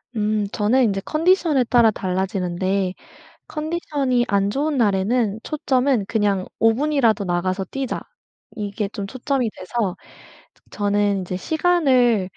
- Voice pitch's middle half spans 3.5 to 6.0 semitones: Yes, average, 5.2 semitones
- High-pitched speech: Yes, high, 220 Hz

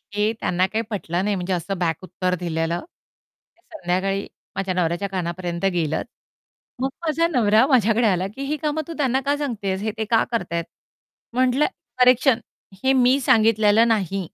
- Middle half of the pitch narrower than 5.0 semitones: No, wide, 5.6 semitones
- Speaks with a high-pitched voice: Yes, high, 210 Hz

